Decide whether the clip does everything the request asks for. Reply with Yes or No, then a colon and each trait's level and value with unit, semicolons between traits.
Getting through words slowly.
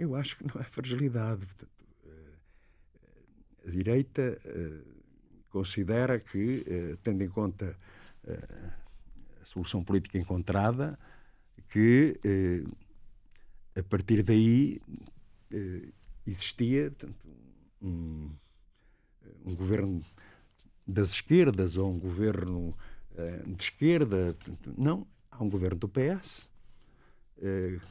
Yes: slow, 80 wpm